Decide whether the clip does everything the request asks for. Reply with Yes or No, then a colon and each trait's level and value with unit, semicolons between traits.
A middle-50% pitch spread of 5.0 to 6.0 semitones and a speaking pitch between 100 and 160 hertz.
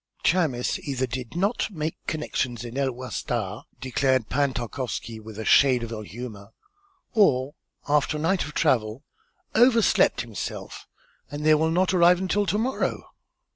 Yes: wide, 5.6 semitones; low, 135 Hz